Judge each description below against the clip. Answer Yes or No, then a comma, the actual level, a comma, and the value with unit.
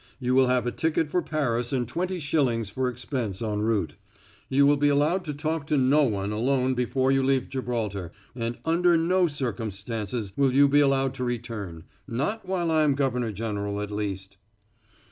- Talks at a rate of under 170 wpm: No, average, 185 wpm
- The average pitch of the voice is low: Yes, low, 130 Hz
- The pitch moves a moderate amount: Yes, average, 4.4 semitones